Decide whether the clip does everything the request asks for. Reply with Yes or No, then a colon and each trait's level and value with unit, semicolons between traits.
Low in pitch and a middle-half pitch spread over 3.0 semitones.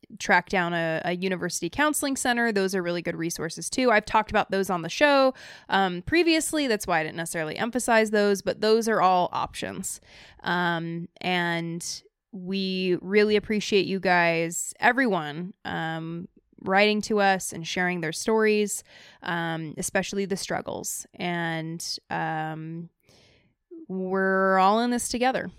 No: high, 190 Hz; average, 4.0 semitones